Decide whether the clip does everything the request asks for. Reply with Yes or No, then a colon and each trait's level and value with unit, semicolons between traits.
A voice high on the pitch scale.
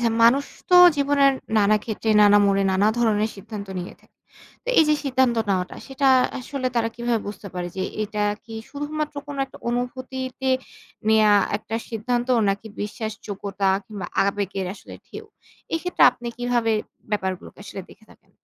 Yes: high, 225 Hz